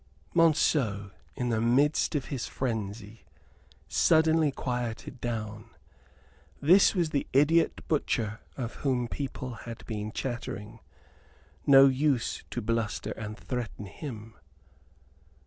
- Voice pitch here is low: Yes, low, 120 Hz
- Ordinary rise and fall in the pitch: Yes, average, 4.2 semitones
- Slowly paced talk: Yes, slow, 110 wpm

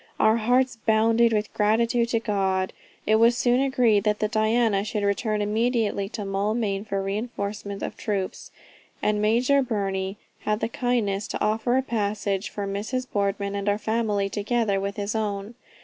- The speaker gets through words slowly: No, average, 165 wpm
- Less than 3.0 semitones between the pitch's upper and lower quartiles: Yes, narrow, 2.5 semitones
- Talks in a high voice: Yes, high, 215 Hz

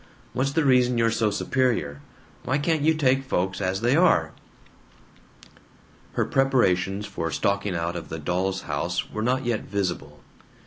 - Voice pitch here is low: Yes, low, 105 Hz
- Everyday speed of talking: Yes, average, 150 wpm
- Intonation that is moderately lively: No, wide, 6.6 semitones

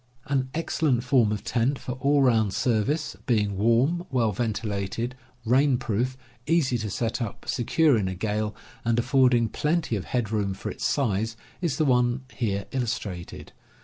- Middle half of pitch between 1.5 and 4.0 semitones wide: Yes, average, 3.7 semitones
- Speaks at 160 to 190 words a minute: Yes, average, 175 wpm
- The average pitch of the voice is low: Yes, low, 120 Hz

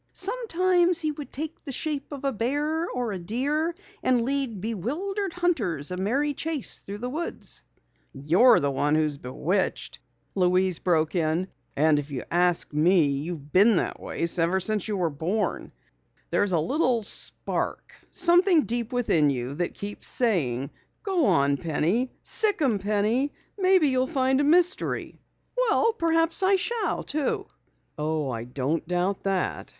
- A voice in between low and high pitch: No, high, 220 Hz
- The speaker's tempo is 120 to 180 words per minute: Yes, average, 155 wpm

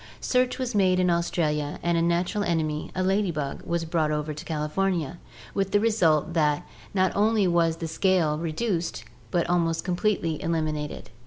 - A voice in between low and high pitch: Yes, medium, 170 Hz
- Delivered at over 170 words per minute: No, average, 165 wpm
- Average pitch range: Yes, average, 3.3 semitones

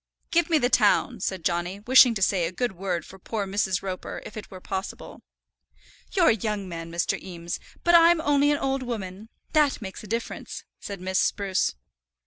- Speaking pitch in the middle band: No, high, 200 Hz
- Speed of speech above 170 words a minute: Yes, average, 190 wpm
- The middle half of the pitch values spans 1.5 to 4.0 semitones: No, wide, 5.5 semitones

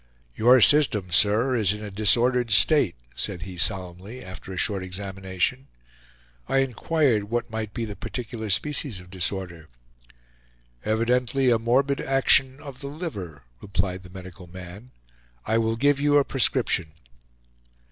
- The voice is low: Yes, low, 110 Hz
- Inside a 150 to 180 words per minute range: No, average, 140 wpm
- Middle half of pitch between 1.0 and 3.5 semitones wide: No, wide, 5.6 semitones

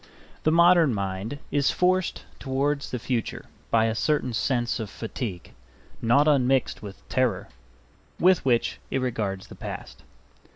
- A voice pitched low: Yes, low, 125 Hz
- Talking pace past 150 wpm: No, slow, 135 wpm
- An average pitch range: Yes, average, 4.6 semitones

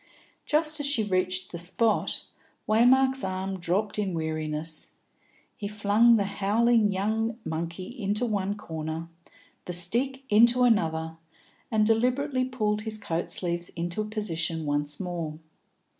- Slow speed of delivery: Yes, slow, 130 wpm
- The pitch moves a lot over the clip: No, average, 5.0 semitones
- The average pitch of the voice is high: Yes, high, 200 Hz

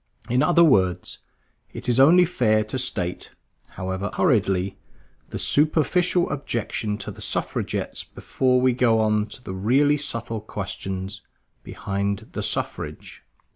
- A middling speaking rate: No, slow, 130 wpm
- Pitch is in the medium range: No, low, 110 Hz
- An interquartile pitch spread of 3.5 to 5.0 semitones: No, wide, 5.5 semitones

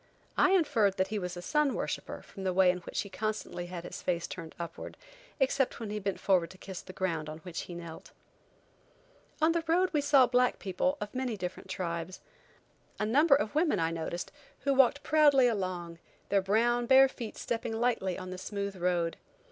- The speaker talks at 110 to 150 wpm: No, average, 195 wpm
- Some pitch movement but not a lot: No, wide, 6.3 semitones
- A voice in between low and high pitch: No, high, 200 Hz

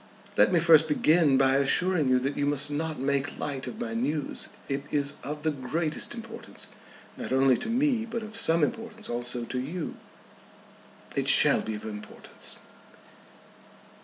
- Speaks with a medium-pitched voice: Yes, medium, 150 Hz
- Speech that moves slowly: No, average, 160 wpm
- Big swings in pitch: Yes, wide, 6.9 semitones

